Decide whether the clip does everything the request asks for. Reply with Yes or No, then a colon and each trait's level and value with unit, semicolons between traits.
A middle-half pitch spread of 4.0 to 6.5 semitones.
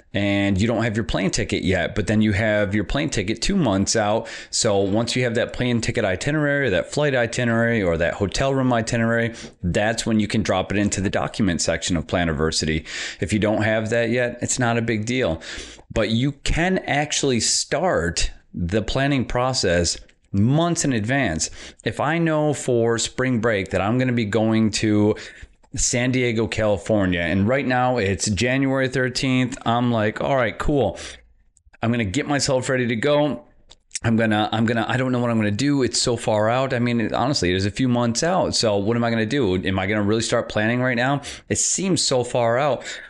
No: average, 3.2 semitones